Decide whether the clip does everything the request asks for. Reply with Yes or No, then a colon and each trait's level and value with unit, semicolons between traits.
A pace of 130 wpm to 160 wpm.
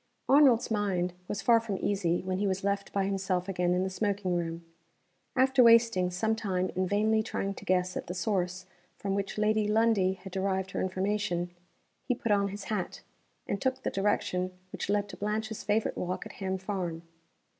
No: average, 190 wpm